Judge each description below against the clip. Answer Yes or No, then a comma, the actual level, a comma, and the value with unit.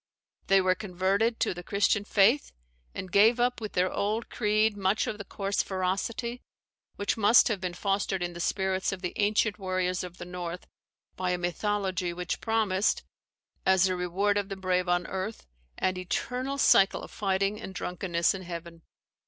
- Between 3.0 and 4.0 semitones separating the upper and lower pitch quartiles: No, narrow, 2.4 semitones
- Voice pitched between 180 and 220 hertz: Yes, high, 190 Hz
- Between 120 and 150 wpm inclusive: No, average, 175 wpm